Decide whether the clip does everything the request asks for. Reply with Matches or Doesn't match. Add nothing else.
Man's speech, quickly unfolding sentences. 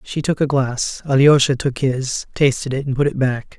Matches